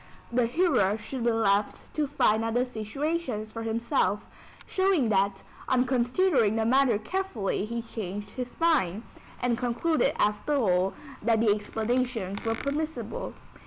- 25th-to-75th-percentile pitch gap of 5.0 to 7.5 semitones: No, average, 4.2 semitones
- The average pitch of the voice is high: Yes, high, 230 Hz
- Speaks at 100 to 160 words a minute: Yes, average, 140 wpm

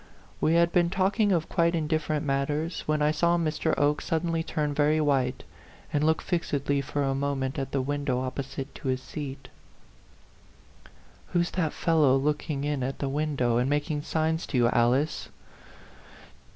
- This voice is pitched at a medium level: Yes, medium, 150 Hz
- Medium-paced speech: Yes, average, 160 wpm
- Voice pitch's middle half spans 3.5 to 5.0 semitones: No, average, 2.7 semitones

